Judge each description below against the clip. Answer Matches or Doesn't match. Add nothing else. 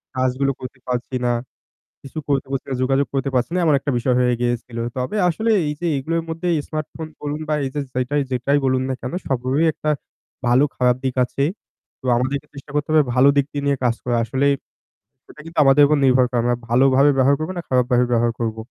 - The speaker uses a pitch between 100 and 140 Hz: Matches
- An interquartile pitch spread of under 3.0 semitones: Matches